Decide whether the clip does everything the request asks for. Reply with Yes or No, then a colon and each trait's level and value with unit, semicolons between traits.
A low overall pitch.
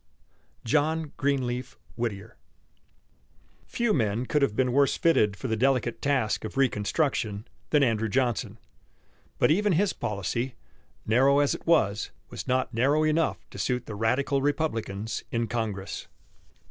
Yes: low, 125 Hz